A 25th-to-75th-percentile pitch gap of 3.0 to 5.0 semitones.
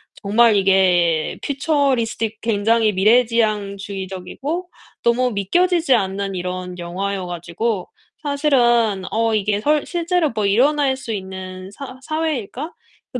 No: wide, 5.6 semitones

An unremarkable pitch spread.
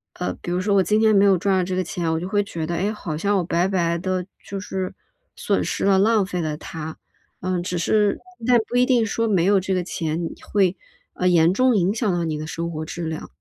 Yes: average, 3.0 semitones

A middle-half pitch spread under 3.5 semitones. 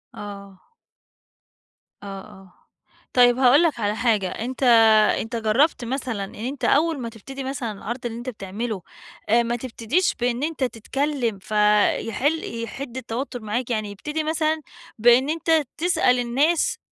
No: average, 4.1 semitones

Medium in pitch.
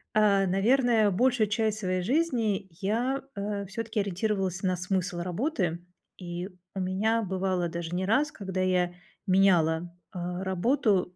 No: high, 195 Hz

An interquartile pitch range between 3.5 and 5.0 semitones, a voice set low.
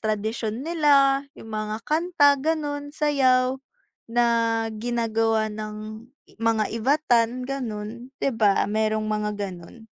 No: average, 4.2 semitones; high, 230 Hz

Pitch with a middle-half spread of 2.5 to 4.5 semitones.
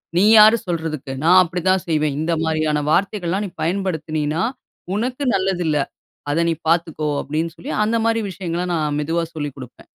Yes: average, 3.4 semitones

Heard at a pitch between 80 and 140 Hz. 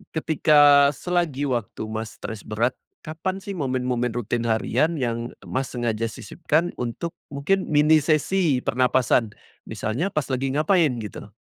Yes: low, 135 Hz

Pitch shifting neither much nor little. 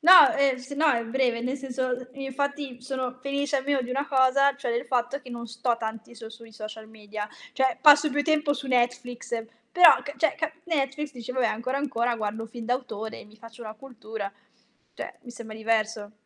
Yes: average, 3.4 semitones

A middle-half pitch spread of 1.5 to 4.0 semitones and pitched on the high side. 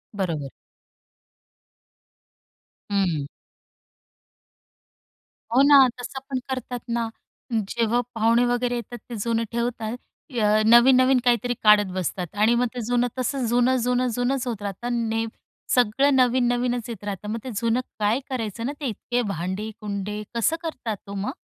Yes: average, 2.8 semitones; high, 235 Hz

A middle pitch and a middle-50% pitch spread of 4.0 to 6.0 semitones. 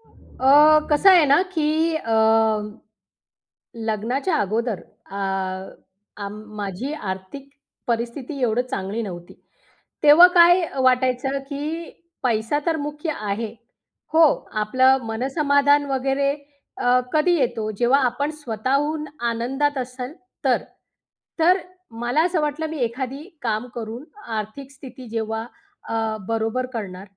No: very high, 255 Hz; average, 4.4 semitones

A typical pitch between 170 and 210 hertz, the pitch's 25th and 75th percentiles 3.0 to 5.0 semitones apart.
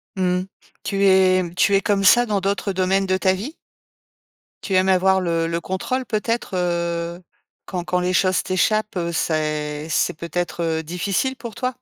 No: medium, 185 Hz; narrow, 2.6 semitones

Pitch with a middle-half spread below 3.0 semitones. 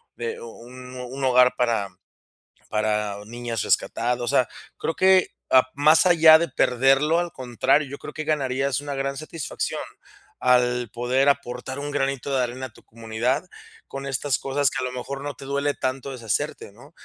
Yes: narrow, 2.6 semitones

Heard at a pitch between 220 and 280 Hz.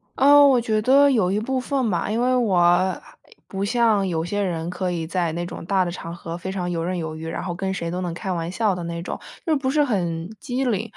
No: high, 190 Hz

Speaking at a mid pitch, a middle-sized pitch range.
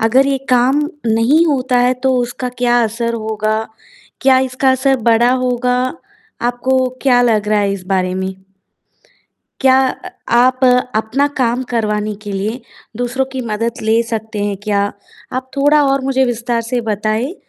No: high, 240 Hz; average, 3.0 semitones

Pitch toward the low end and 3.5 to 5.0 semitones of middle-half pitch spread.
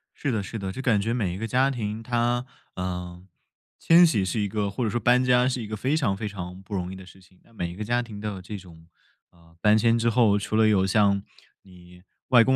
Yes: low, 105 Hz; average, 4.0 semitones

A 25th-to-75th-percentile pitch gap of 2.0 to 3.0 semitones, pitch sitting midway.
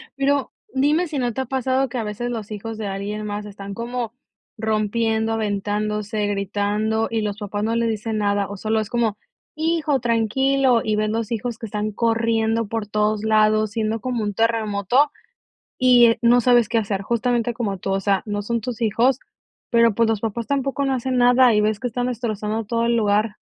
No: narrow, 2.4 semitones; high, 225 Hz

